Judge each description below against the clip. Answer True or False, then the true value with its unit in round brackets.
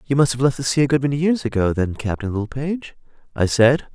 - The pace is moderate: False (245 wpm)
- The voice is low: True (130 Hz)